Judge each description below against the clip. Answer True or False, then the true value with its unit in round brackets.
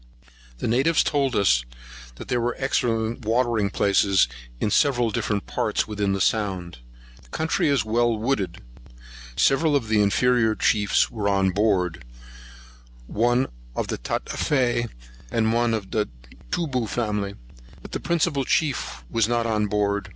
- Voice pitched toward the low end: True (110 Hz)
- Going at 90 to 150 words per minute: True (140 wpm)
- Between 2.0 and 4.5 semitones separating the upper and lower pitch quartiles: True (3.5 semitones)